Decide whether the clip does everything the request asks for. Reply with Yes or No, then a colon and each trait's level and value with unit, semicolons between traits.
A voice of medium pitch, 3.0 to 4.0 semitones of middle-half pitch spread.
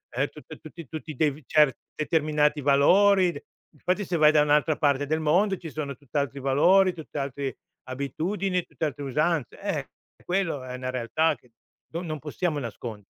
Yes: medium, 150 Hz; average, 3.3 semitones